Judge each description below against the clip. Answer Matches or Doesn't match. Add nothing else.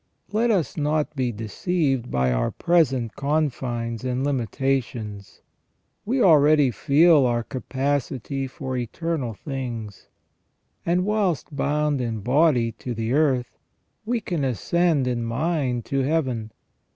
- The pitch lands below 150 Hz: Matches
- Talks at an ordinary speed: Doesn't match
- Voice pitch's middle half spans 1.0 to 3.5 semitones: Doesn't match